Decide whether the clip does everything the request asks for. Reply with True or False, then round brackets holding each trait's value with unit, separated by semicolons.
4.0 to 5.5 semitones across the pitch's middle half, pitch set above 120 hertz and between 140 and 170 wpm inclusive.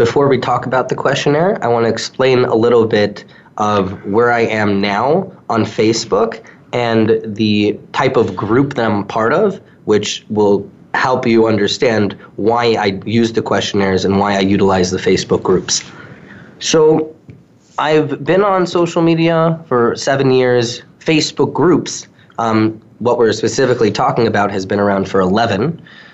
False (5.2 semitones; 115 Hz; 155 wpm)